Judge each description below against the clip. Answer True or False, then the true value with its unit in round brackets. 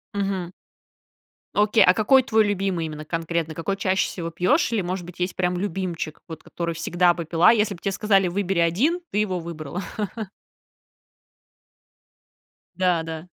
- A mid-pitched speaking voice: True (180 Hz)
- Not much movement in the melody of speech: False (3.0 semitones)